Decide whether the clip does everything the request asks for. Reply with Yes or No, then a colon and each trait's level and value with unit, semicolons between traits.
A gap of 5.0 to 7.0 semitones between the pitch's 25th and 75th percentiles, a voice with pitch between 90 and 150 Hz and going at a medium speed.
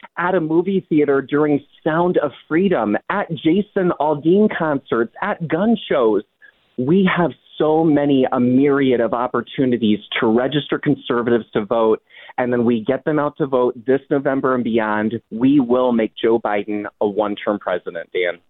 Yes: wide, 5.6 semitones; medium, 140 Hz; average, 160 wpm